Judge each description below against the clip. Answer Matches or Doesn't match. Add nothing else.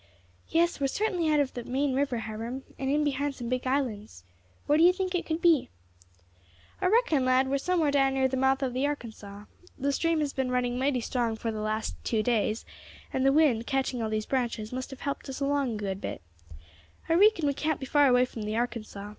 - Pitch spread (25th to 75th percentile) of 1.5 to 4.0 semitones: Matches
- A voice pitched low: Doesn't match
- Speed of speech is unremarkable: Doesn't match